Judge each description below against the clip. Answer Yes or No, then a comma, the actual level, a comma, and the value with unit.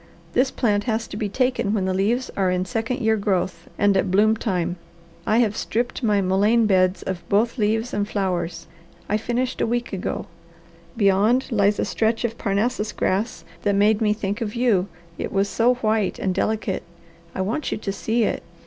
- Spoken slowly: No, average, 190 wpm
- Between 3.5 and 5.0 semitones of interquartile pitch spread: No, average, 2.7 semitones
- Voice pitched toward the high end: Yes, high, 210 Hz